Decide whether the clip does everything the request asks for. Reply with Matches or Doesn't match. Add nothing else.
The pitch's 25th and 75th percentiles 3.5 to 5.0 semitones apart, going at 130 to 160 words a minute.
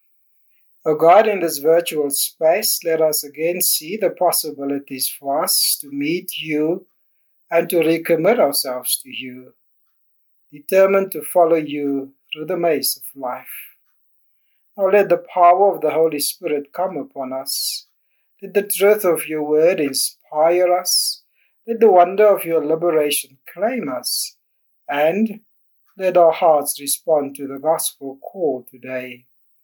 Matches